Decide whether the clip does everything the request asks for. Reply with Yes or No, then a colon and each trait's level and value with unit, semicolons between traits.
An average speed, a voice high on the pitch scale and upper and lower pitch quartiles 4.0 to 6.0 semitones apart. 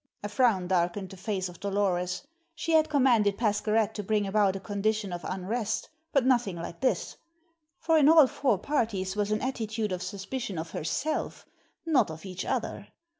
Yes: average, 175 wpm; high, 205 Hz; average, 4.3 semitones